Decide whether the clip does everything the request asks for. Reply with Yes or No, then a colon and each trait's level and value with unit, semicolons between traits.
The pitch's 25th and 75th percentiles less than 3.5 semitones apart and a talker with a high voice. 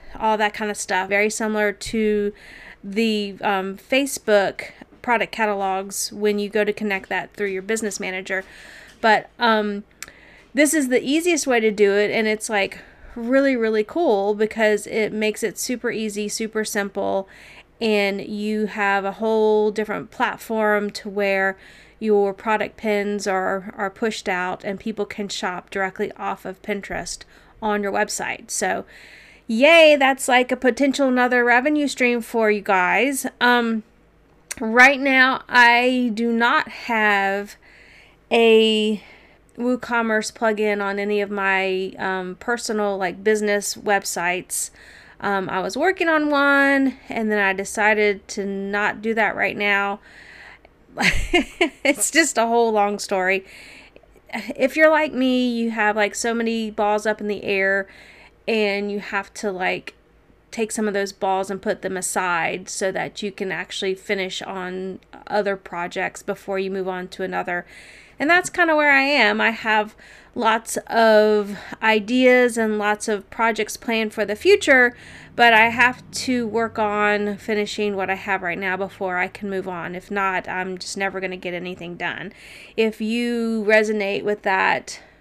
Yes: average, 2.7 semitones; high, 210 Hz